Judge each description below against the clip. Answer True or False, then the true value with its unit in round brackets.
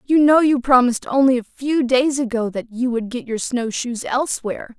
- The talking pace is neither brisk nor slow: False (215 wpm)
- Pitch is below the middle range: False (250 Hz)